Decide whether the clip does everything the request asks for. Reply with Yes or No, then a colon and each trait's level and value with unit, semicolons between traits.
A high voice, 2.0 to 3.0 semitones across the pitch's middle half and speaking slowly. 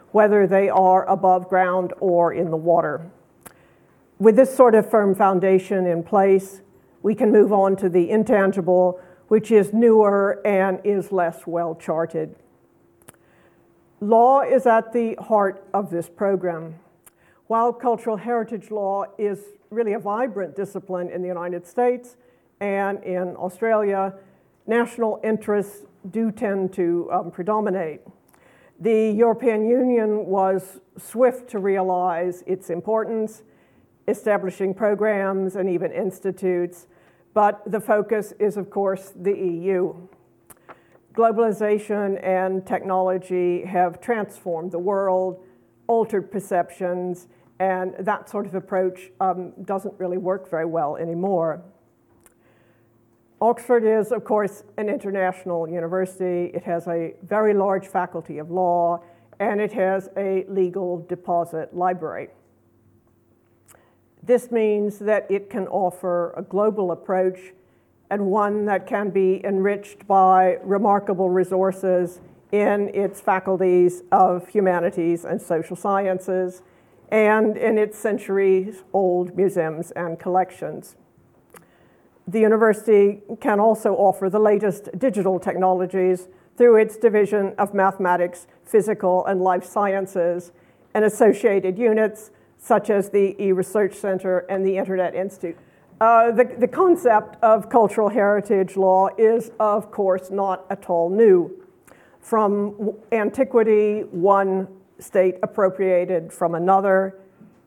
Yes: high, 195 Hz; narrow, 2.6 semitones; slow, 120 wpm